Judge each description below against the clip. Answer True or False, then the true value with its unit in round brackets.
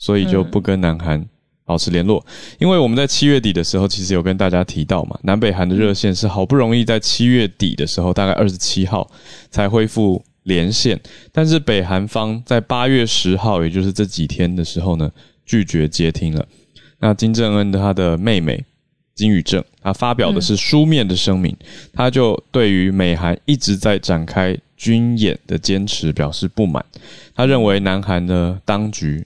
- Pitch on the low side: True (100 Hz)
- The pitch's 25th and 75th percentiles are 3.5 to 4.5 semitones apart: True (4.1 semitones)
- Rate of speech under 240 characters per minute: False (275 characters per minute)